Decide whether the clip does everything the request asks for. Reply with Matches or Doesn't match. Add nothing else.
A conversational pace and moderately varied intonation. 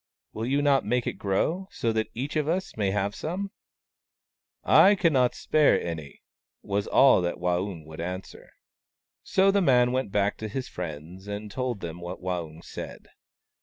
Doesn't match